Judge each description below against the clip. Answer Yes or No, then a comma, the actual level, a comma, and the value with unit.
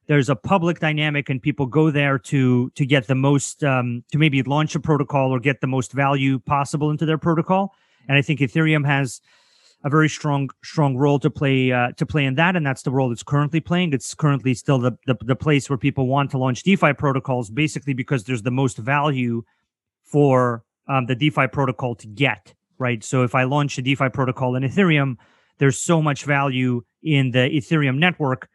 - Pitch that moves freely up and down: No, narrow, 2.6 semitones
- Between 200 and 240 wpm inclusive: Yes, fast, 205 wpm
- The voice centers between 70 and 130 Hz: No, medium, 140 Hz